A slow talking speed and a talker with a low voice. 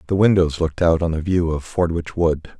No: fast, 230 wpm; very low, 85 Hz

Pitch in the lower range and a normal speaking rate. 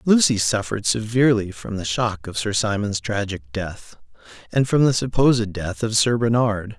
Yes: low, 110 Hz; average, 170 wpm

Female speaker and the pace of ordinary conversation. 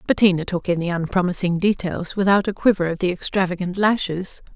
Yes: female; average, 170 wpm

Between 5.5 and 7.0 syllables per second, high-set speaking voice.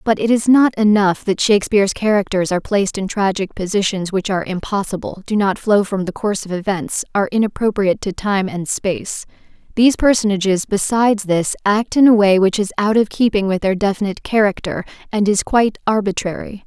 Yes: 5.8 syllables/s; high, 200 Hz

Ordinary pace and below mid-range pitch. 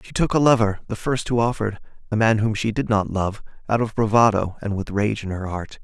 No: fast, 245 wpm; low, 105 Hz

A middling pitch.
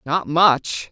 Yes: medium, 160 Hz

